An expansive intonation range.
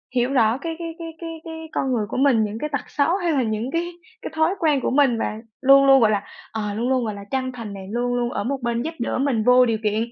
No: average, 4.6 semitones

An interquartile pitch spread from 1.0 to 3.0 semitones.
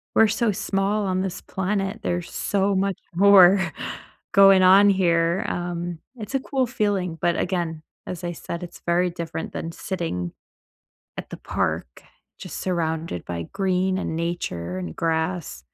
Yes: average, 2.7 semitones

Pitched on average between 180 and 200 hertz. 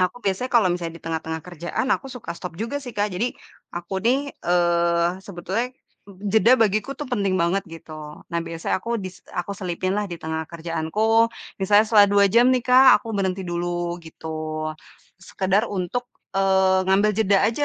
Yes: high, 190 Hz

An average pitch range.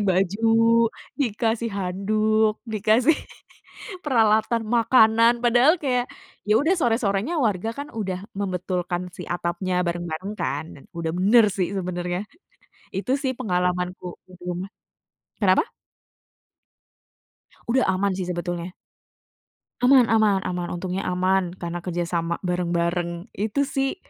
Yes: average, 4.2 semitones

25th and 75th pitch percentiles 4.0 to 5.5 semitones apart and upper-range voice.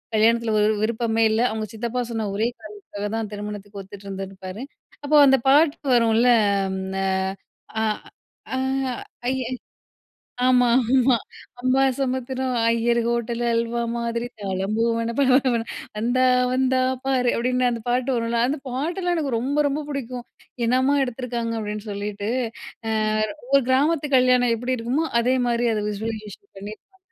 No: average, 2.8 semitones; high, 235 Hz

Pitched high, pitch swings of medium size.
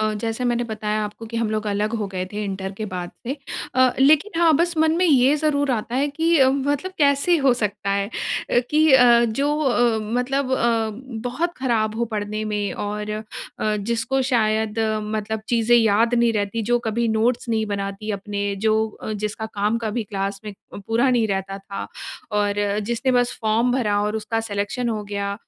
Yes: high, 225 Hz; average, 3.3 semitones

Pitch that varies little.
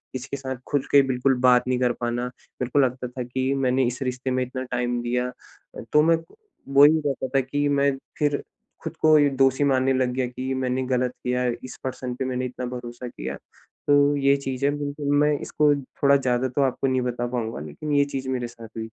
Yes: narrow, 1.9 semitones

